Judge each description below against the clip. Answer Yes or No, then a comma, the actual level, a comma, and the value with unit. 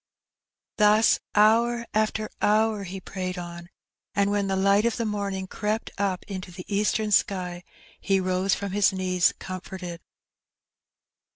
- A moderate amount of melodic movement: No, narrow, 2.3 semitones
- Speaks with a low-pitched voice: No, high, 200 Hz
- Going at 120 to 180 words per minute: Yes, slow, 135 wpm